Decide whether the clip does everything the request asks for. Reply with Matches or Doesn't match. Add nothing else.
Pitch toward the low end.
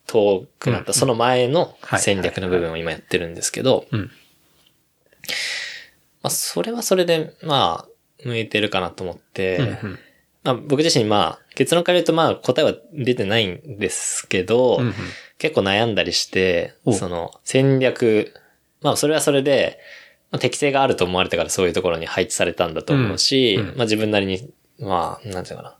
Matches